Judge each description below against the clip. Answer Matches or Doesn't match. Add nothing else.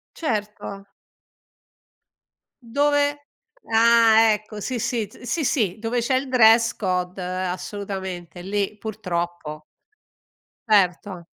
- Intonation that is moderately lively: Matches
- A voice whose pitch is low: Doesn't match